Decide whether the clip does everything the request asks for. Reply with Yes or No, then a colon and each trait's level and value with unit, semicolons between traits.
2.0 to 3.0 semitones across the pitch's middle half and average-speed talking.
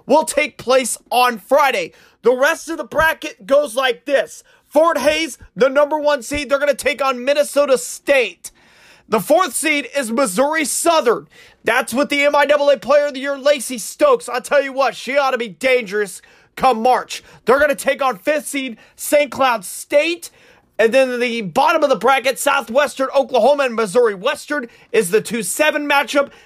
Yes: narrow, 2.6 semitones; average, 175 wpm